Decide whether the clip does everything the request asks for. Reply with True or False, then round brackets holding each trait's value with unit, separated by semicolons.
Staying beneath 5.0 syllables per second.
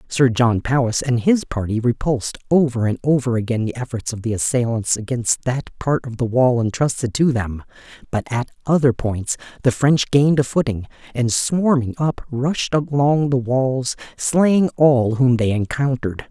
True (4.6 syllables/s)